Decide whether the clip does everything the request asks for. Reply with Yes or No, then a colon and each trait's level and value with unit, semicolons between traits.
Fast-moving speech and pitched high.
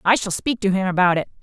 Yes: fast, 295 wpm; high, 195 Hz